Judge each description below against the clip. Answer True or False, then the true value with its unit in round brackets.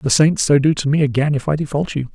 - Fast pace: True (310 wpm)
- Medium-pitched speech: True (145 Hz)